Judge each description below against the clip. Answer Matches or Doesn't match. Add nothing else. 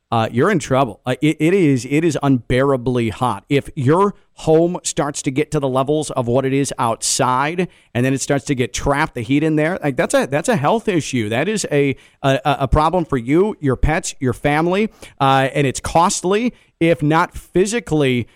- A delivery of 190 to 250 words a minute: Matches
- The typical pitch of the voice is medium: Matches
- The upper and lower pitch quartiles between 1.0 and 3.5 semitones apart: Doesn't match